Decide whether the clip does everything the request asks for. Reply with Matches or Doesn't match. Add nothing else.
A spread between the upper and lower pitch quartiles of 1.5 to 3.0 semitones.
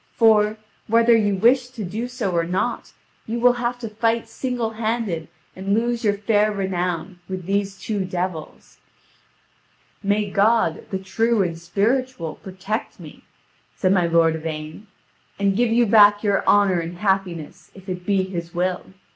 Doesn't match